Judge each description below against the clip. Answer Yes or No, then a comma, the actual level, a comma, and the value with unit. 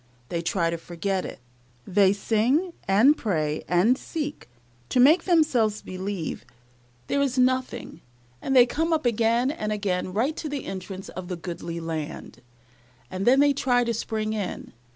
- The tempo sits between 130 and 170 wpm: Yes, average, 160 wpm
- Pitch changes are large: Yes, wide, 6.2 semitones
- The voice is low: No, high, 215 Hz